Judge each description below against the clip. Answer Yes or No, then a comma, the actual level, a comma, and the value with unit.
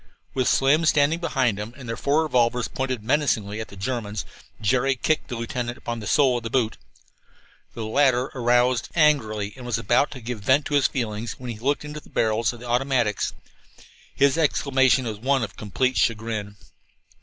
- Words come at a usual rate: Yes, average, 185 wpm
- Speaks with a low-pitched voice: Yes, low, 125 Hz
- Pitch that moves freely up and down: No, average, 3.3 semitones